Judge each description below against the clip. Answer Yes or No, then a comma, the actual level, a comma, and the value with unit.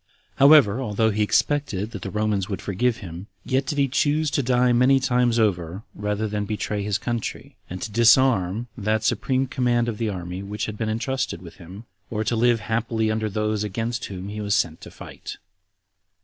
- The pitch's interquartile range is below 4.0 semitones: Yes, average, 3.2 semitones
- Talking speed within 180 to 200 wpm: Yes, average, 195 wpm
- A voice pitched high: No, low, 110 Hz